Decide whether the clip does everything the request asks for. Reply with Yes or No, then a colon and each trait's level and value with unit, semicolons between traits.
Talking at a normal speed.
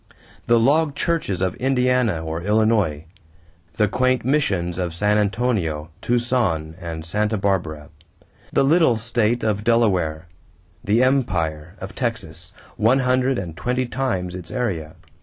No: slow, 130 wpm